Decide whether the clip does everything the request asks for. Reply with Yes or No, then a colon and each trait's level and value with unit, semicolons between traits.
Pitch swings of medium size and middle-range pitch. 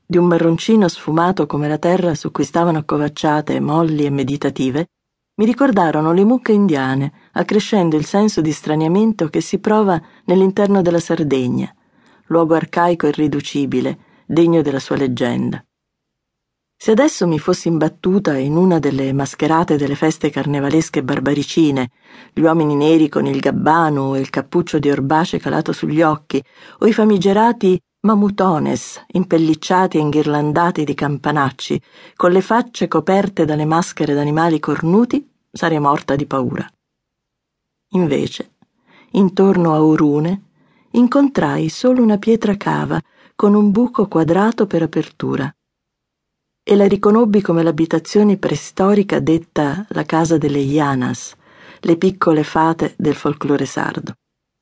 Yes: average, 4.6 semitones; medium, 165 Hz